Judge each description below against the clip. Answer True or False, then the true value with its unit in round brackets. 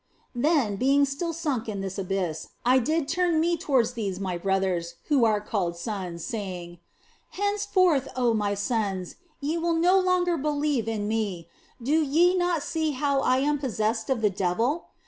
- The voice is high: True (245 Hz)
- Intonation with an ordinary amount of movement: False (7.6 semitones)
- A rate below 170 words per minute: False (175 wpm)